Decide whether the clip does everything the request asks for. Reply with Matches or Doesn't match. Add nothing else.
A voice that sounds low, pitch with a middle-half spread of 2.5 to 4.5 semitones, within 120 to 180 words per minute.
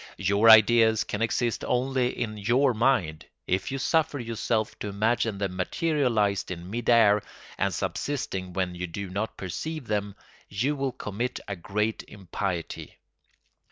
Matches